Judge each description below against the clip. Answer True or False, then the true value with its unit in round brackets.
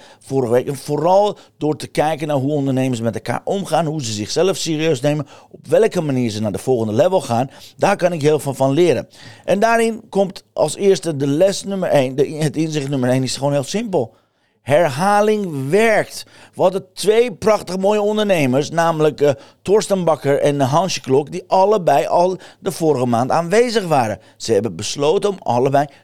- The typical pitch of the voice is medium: True (155 Hz)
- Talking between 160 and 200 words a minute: True (185 wpm)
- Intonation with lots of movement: True (5.9 semitones)